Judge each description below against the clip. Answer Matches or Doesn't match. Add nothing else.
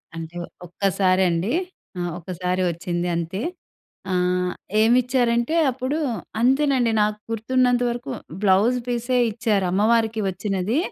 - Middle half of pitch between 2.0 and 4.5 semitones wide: Doesn't match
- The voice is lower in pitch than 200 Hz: Doesn't match